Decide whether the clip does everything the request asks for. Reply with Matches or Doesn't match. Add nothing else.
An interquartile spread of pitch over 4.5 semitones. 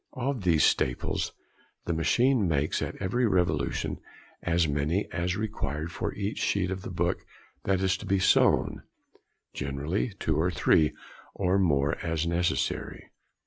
Doesn't match